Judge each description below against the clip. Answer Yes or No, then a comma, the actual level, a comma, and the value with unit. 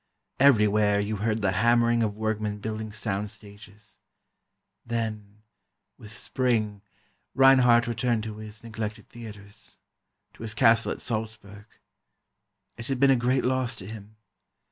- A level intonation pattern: Yes, narrow, 2.1 semitones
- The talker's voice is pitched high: No, low, 110 Hz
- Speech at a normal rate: No, slow, 120 wpm